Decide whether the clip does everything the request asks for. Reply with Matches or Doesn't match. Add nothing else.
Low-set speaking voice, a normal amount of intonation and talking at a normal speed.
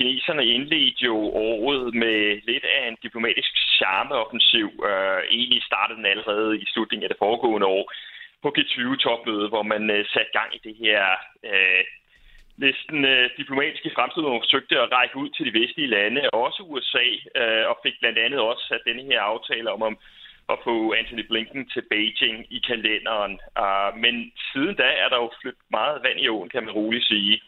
Matches